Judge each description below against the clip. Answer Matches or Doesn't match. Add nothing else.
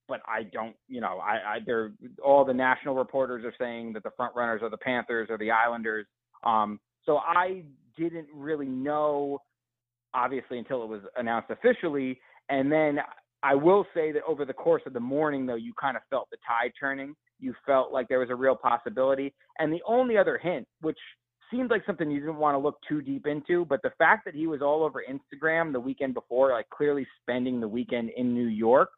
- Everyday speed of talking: Doesn't match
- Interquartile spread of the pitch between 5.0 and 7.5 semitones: Doesn't match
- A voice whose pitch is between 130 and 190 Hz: Matches